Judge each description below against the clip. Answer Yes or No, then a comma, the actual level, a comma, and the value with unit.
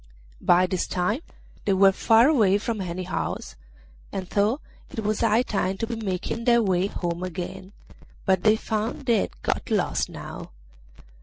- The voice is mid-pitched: No, high, 200 Hz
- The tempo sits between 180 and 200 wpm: No, average, 165 wpm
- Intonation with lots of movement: No, average, 3.4 semitones